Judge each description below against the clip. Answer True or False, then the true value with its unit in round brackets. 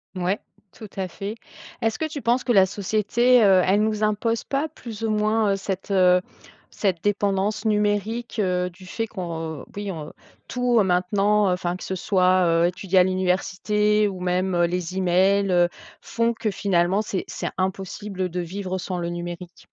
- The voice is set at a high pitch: True (195 Hz)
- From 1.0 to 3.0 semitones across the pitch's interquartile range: True (2.7 semitones)